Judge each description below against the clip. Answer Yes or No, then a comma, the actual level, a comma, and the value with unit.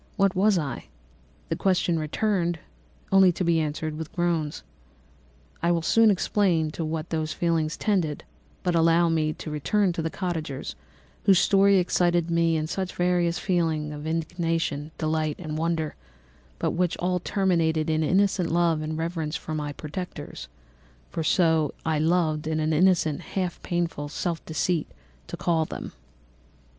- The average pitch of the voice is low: No, medium, 165 Hz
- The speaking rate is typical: Yes, average, 155 wpm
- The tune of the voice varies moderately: No, narrow, 2.3 semitones